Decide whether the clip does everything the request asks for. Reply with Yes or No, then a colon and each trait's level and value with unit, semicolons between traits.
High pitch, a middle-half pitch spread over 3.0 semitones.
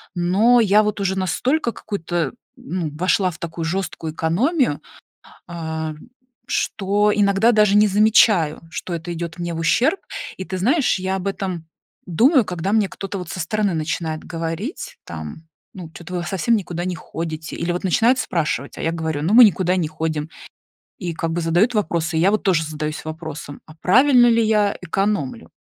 No: medium, 180 Hz; average, 4.4 semitones